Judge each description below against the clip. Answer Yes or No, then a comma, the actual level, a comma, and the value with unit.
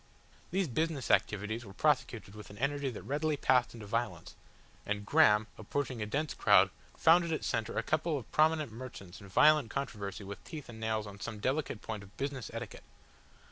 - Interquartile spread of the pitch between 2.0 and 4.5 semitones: No, wide, 5.6 semitones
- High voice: No, low, 115 Hz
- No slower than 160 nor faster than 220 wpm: Yes, average, 185 wpm